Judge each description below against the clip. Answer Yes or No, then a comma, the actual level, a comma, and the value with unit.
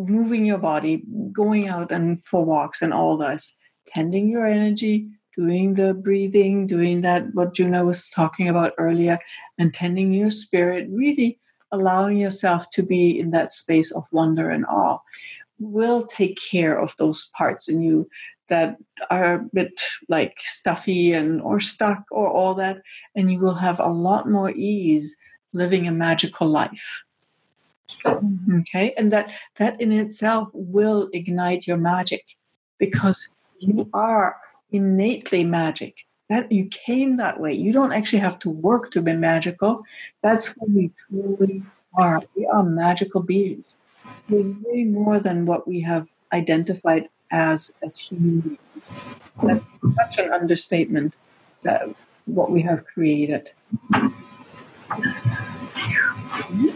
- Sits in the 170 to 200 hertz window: Yes, high, 190 Hz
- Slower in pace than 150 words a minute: Yes, average, 140 wpm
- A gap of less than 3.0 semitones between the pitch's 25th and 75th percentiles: No, average, 3.6 semitones